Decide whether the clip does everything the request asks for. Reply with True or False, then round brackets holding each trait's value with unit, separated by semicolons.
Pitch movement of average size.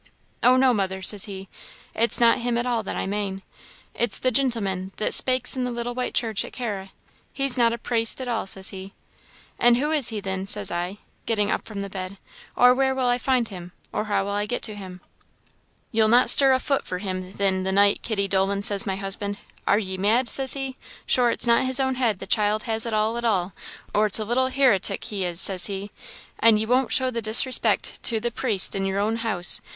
True (3.9 semitones)